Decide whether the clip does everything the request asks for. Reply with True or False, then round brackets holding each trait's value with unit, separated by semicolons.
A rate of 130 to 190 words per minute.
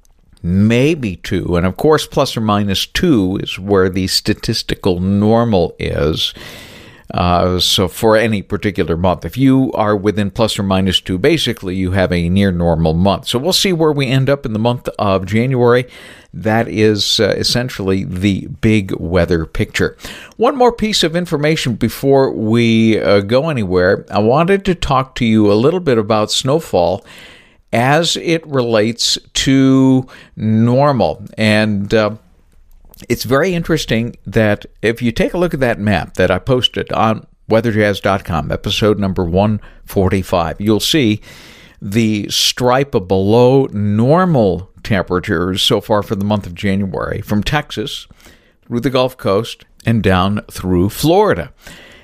True (150 wpm)